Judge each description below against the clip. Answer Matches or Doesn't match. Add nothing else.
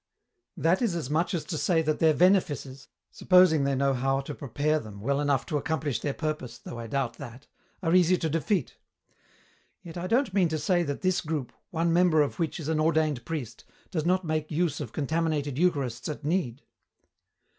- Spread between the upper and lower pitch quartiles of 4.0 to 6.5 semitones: Doesn't match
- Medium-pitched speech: Matches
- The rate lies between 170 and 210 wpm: Matches